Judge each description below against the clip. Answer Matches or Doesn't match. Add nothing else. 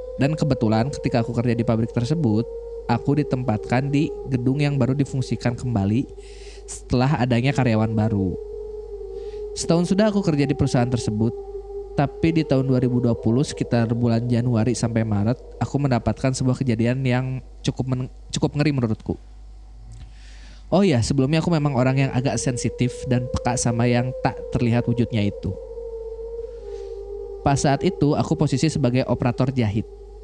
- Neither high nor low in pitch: Doesn't match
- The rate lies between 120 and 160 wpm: Matches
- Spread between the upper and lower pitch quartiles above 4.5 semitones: Matches